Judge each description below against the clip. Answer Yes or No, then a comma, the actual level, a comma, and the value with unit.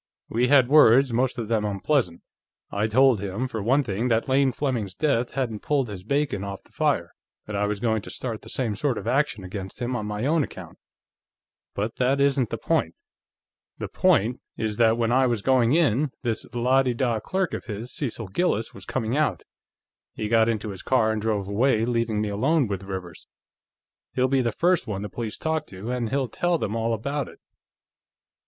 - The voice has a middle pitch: No, low, 115 Hz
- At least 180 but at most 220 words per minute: Yes, average, 200 wpm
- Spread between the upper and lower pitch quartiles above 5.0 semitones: No, average, 3.9 semitones